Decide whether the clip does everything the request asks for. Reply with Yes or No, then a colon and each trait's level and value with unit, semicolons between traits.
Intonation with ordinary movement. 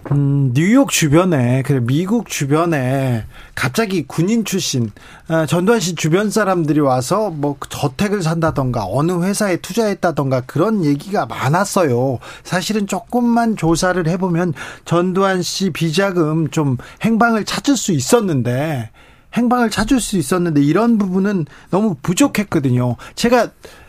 No: wide, 6.2 semitones